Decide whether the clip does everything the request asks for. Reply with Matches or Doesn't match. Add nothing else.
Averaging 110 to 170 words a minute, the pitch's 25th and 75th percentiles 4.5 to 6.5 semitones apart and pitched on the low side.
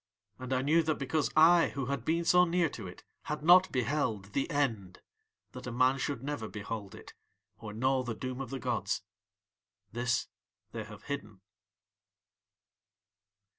Matches